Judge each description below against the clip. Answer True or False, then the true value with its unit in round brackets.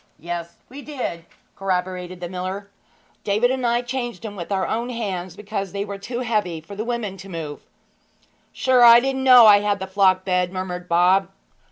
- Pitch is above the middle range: True (200 Hz)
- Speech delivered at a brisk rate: False (185 wpm)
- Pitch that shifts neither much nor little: True (4.4 semitones)